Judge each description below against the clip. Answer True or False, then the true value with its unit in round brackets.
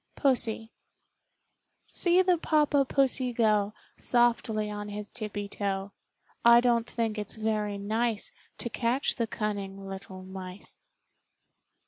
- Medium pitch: False (220 Hz)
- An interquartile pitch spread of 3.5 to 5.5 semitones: False (2.9 semitones)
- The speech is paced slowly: True (120 wpm)